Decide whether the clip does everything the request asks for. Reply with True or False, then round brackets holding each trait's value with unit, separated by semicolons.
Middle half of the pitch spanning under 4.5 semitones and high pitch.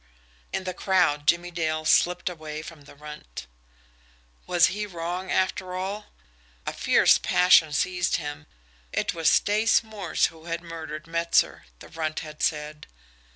False (2.8 semitones; 165 Hz)